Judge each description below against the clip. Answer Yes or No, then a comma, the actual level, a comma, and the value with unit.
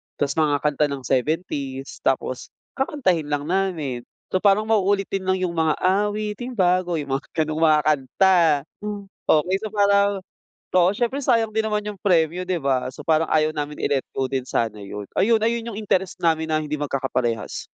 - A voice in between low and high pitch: Yes, medium, 170 Hz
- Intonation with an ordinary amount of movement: No, wide, 5.8 semitones